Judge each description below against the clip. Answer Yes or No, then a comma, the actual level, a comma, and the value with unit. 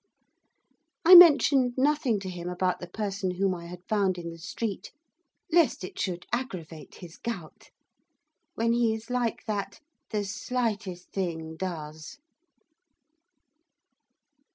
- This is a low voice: No, high, 195 Hz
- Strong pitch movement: No, average, 5.0 semitones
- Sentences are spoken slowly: Yes, slow, 125 wpm